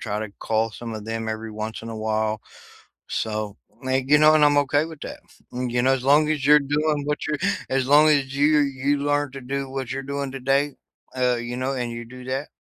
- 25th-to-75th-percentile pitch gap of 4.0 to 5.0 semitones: No, average, 3.6 semitones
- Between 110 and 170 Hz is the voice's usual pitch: Yes, low, 135 Hz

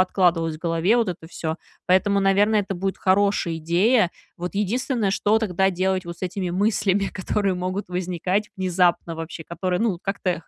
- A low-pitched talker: No, medium, 185 Hz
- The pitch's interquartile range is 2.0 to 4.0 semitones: Yes, narrow, 2.4 semitones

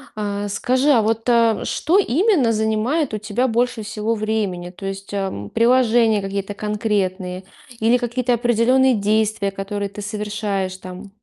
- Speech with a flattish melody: No, average, 3.1 semitones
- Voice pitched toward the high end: Yes, high, 215 Hz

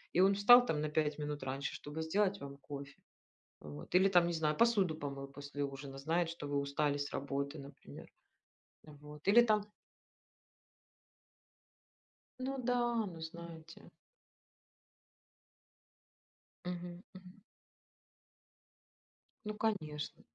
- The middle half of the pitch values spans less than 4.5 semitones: No, average, 5.1 semitones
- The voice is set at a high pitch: No, medium, 160 Hz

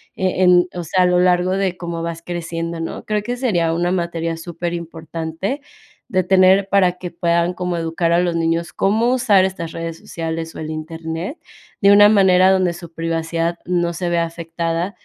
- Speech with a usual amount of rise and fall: No, narrow, 2.0 semitones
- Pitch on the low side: No, medium, 175 Hz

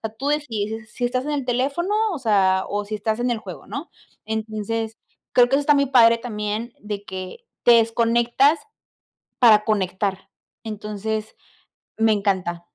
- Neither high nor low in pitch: No, high, 220 Hz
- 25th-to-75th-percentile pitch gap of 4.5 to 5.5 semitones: No, average, 2.8 semitones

